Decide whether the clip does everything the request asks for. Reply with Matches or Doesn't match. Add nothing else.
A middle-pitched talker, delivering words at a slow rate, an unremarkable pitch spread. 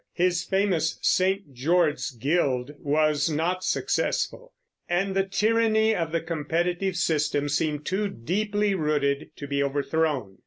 Matches